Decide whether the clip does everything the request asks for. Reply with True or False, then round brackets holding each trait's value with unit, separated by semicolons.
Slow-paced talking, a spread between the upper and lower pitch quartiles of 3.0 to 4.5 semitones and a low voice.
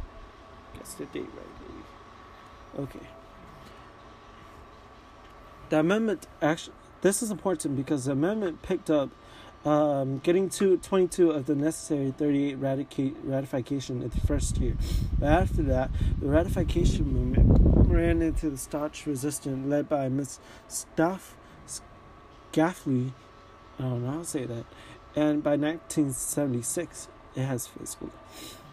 False (125 wpm; 3.6 semitones; 145 Hz)